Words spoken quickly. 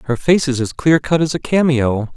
Yes: fast, 250 wpm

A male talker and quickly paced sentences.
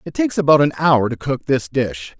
Yes: male; fast, 245 wpm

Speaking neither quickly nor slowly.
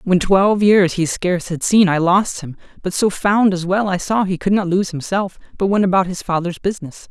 No: fast, 235 wpm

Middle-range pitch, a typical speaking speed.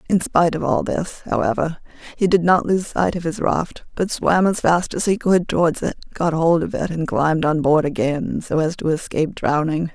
No: medium, 165 Hz; fast, 225 wpm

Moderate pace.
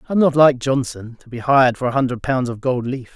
No: fast, 285 wpm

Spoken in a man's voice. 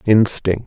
Yes: male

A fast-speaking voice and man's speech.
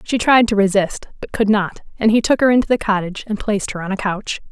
No: fast, 265 wpm; female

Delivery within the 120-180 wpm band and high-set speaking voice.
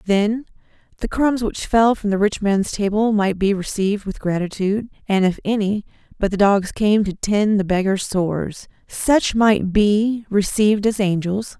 Yes: average, 170 wpm; high, 205 Hz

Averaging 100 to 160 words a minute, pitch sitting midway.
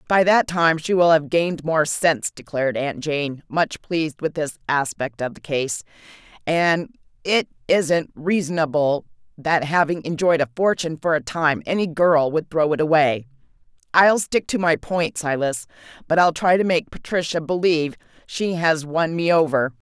No: average, 170 wpm; medium, 160 Hz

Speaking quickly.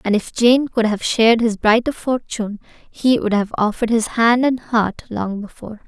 No: average, 195 wpm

